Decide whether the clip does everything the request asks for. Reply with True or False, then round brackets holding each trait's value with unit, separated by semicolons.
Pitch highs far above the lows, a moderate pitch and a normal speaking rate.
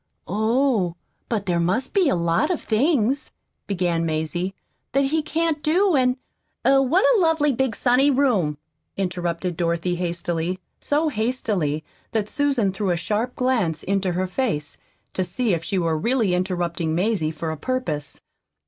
False (7.5 semitones; 200 Hz; 155 wpm)